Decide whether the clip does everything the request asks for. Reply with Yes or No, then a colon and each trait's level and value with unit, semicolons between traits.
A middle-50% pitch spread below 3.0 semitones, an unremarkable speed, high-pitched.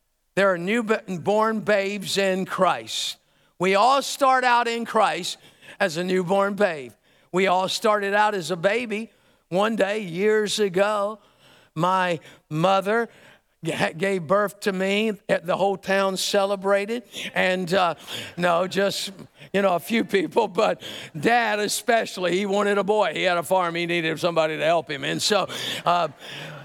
Yes: narrow, 2.5 semitones; average, 150 wpm; high, 195 Hz